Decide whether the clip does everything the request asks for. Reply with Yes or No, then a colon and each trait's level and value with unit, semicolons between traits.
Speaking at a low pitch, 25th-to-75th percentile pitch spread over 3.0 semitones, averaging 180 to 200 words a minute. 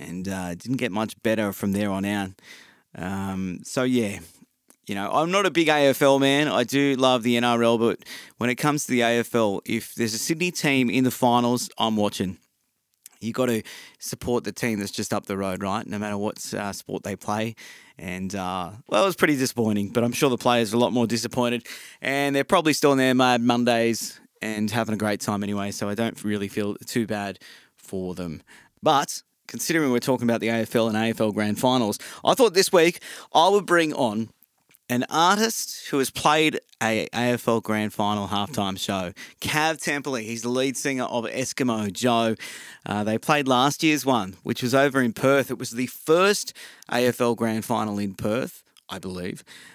Yes: low, 115 Hz; average, 4.0 semitones; average, 195 wpm